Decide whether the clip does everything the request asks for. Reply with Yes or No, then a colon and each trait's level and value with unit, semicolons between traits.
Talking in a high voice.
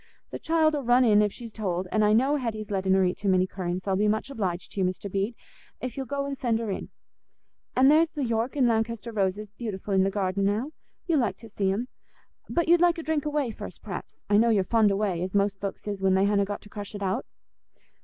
Yes: high, 210 Hz